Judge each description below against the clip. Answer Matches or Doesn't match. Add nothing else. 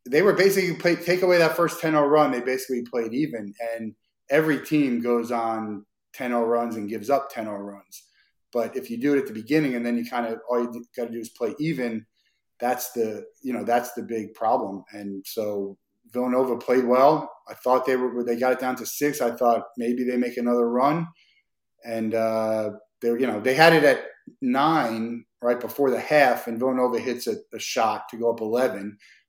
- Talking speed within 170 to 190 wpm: Doesn't match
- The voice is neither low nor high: Doesn't match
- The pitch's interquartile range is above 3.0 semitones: Doesn't match